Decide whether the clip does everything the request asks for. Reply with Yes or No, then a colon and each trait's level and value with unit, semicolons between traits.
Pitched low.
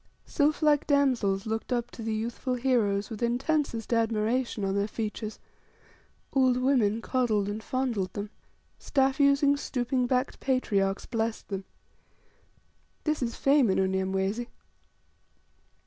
No: high, 235 Hz